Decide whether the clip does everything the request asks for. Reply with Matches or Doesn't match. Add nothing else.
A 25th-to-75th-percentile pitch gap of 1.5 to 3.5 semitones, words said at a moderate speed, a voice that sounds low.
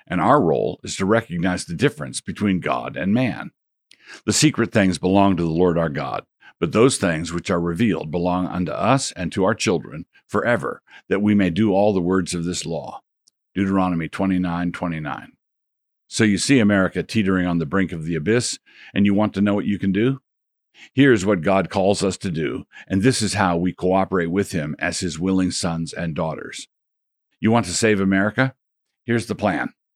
Matches